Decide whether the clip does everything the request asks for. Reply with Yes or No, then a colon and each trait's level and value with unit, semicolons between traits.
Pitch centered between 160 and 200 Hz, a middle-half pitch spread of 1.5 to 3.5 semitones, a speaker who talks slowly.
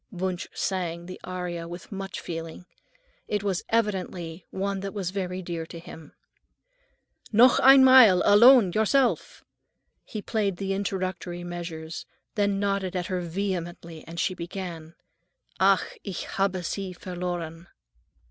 Yes: medium, 185 Hz; narrow, 2.4 semitones; slow, 130 wpm